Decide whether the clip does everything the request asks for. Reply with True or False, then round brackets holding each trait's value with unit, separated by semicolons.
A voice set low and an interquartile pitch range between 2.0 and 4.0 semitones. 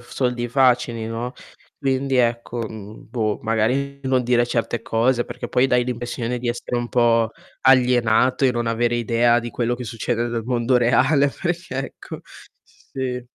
False (120 Hz; 1.6 semitones)